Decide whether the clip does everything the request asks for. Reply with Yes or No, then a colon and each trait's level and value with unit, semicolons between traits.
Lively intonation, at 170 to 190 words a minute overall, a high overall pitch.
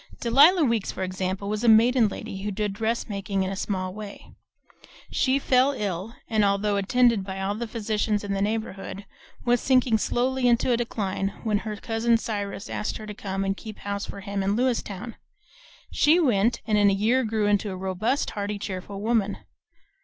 No: average, 2.9 semitones; average, 185 wpm; high, 210 Hz